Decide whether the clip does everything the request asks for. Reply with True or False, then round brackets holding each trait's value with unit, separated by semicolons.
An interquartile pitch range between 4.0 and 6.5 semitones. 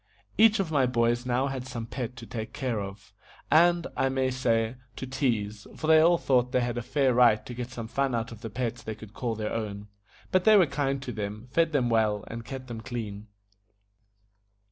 False (3.1 semitones)